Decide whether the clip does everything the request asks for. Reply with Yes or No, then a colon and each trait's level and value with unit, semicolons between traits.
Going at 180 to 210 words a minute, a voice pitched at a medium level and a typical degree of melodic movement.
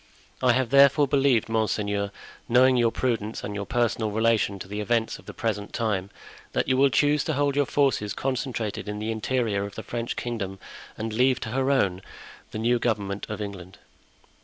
No: average, 185 wpm; low, 115 Hz; average, 3.9 semitones